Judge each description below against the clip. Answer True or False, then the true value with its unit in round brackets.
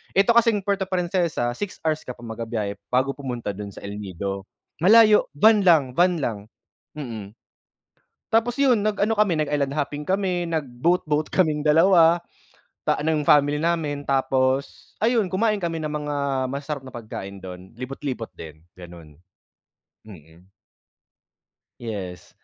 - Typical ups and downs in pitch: False (7.7 semitones)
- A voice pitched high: False (150 Hz)